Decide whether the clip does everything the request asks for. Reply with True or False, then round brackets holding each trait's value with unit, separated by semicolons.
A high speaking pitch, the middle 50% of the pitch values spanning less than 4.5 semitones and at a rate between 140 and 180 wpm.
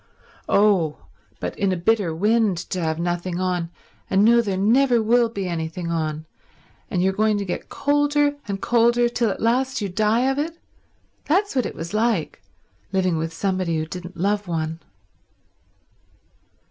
False (200 Hz; 5.2 semitones; 160 wpm)